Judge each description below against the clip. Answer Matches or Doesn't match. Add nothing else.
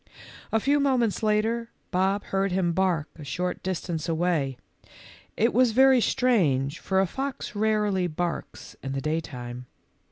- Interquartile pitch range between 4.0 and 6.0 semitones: Matches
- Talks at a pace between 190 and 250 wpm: Doesn't match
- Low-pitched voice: Doesn't match